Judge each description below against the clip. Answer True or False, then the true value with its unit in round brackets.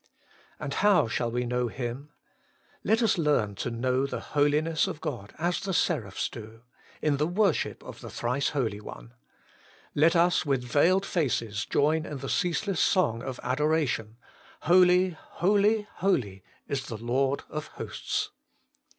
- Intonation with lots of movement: True (6.3 semitones)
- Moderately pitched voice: True (145 Hz)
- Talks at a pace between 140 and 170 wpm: True (150 wpm)